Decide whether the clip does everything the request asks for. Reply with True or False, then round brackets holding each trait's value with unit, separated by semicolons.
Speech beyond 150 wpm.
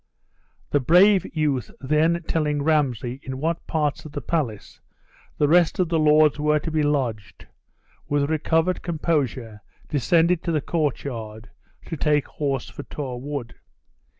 False (145 wpm)